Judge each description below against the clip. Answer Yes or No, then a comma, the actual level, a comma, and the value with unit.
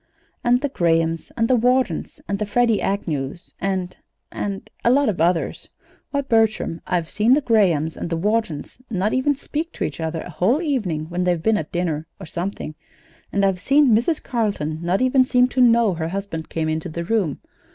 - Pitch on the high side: Yes, high, 195 Hz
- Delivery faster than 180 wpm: Yes, average, 195 wpm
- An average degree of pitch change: No, wide, 6.5 semitones